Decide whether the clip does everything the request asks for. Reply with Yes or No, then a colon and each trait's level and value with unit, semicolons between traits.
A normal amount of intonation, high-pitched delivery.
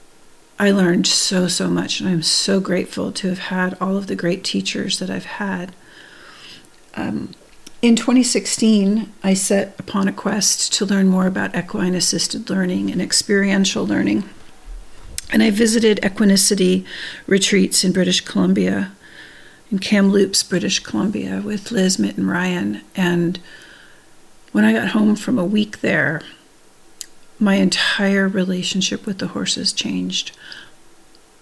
No: narrow, 2.3 semitones; high, 195 Hz